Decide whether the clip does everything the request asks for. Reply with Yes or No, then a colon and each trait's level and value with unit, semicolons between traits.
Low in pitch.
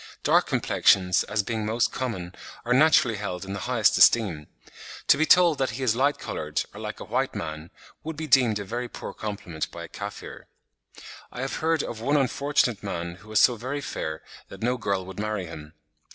Yes: low, 110 Hz